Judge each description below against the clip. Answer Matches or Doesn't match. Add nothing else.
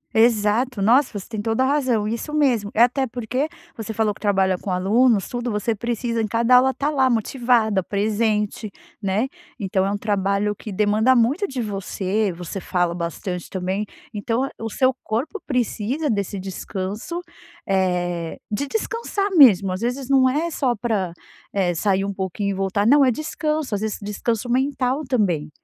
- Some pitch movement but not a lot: Matches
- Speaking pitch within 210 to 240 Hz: Matches